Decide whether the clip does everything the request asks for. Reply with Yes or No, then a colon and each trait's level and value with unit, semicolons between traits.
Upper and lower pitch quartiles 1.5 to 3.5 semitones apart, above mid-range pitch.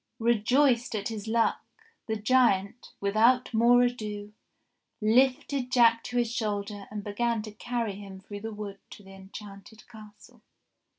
Yes: average, 2.8 semitones; high, 220 Hz